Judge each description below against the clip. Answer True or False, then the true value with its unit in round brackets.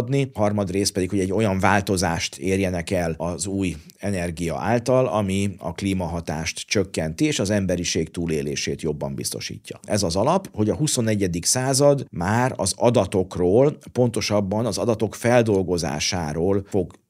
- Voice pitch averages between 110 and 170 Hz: False (100 Hz)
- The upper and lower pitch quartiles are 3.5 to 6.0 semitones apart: True (3.8 semitones)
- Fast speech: False (135 wpm)